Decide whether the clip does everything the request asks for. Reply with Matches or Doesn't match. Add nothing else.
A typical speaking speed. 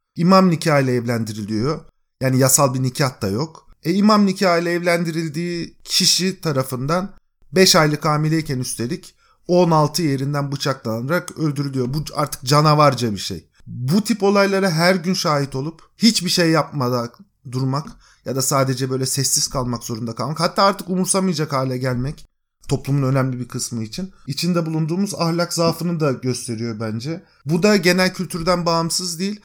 Doesn't match